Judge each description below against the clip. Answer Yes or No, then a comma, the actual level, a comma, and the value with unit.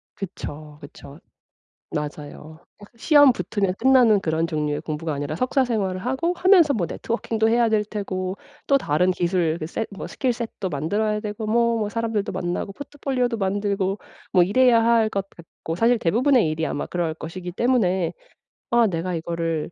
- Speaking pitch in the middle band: No, high, 200 Hz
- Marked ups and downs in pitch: Yes, wide, 5.8 semitones